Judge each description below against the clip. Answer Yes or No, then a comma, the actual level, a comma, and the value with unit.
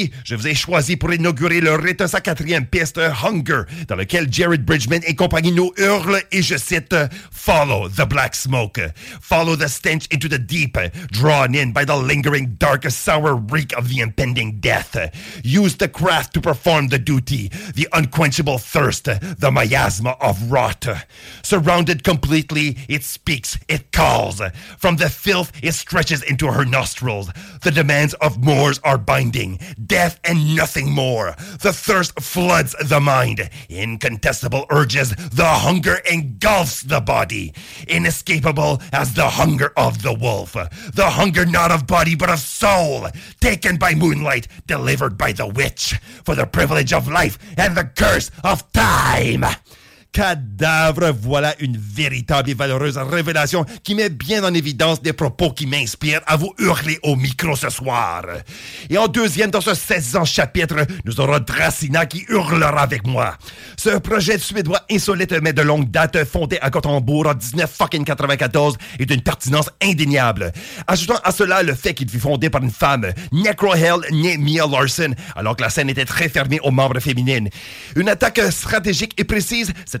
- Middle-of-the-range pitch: Yes, medium, 150 Hz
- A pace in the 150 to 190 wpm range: Yes, average, 160 wpm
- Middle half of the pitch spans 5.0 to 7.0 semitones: No, average, 4.4 semitones